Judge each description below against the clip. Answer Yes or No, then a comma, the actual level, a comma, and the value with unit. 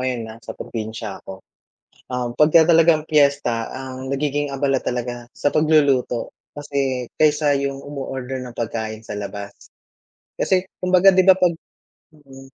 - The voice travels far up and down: No, average, 3.8 semitones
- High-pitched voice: No, low, 135 Hz